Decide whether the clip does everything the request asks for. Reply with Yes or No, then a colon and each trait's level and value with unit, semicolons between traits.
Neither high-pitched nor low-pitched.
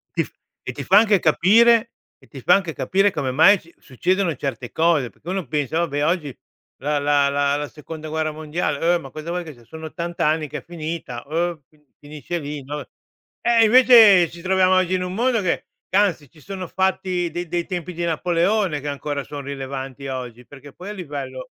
Yes: medium, 160 Hz